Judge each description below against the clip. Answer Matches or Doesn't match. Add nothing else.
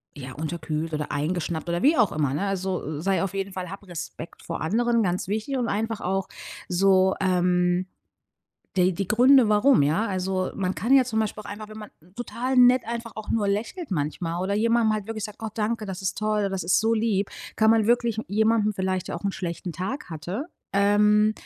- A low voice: Doesn't match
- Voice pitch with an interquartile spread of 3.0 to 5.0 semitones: Matches